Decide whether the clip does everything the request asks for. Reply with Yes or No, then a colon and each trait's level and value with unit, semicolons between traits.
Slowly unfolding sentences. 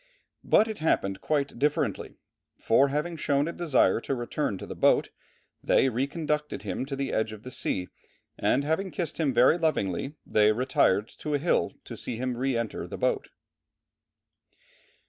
No: average, 165 wpm